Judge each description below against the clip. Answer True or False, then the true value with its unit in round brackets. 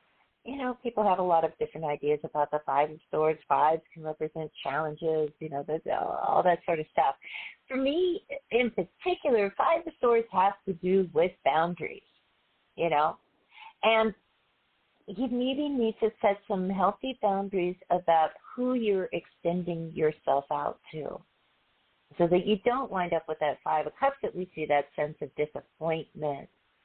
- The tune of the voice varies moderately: False (6.8 semitones)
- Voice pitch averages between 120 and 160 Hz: False (180 Hz)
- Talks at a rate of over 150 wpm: True (165 wpm)